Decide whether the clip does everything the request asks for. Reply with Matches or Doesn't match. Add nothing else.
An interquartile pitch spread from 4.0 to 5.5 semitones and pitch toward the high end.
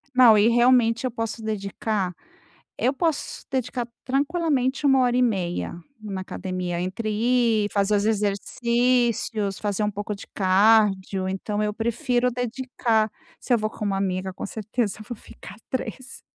Doesn't match